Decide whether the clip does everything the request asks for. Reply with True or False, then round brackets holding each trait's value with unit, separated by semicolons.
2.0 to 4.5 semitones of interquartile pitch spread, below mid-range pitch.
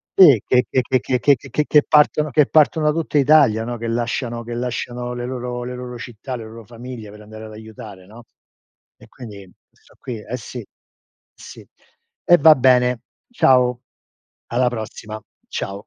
True (2.5 semitones; 120 Hz)